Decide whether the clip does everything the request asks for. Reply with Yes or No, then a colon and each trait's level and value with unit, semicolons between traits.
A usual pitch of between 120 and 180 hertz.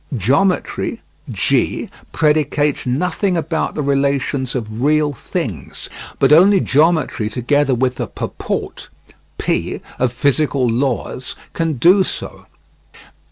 Yes: medium, 140 Hz